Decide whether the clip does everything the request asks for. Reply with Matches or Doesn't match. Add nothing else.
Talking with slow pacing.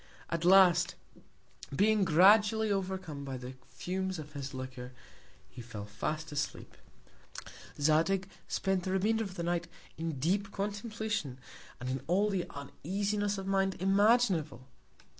Matches